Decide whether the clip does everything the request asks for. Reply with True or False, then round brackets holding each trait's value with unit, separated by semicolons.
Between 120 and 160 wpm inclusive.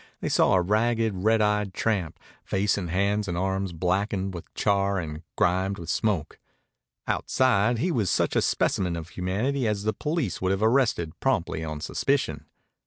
False (170 wpm)